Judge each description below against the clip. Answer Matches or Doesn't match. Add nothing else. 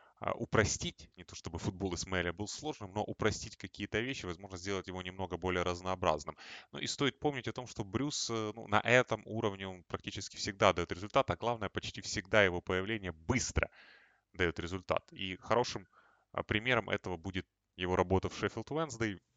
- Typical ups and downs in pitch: Matches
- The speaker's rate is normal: Doesn't match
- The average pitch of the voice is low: Matches